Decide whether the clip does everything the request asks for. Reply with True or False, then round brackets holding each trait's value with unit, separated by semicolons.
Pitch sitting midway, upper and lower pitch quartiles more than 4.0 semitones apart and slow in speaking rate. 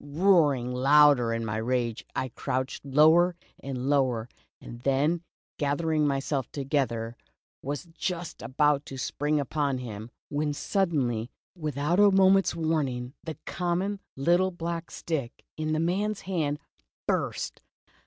True (145 Hz; 4.5 semitones; 125 wpm)